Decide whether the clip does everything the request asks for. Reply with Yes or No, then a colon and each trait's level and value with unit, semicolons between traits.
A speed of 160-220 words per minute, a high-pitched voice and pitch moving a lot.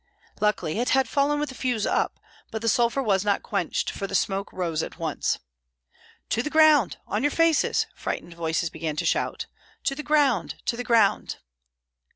Yes: average, 185 wpm; high, 230 Hz; wide, 6.2 semitones